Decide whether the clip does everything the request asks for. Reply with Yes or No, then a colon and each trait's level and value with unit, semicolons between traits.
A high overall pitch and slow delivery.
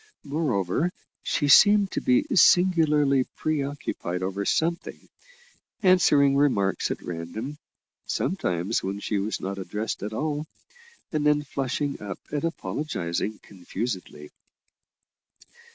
No: medium, 140 Hz; slow, 110 wpm